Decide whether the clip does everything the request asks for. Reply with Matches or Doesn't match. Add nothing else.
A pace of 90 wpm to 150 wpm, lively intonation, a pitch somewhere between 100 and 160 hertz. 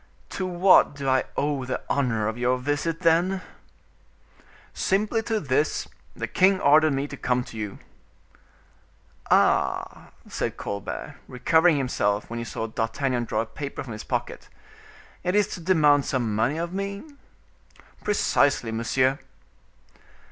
Matches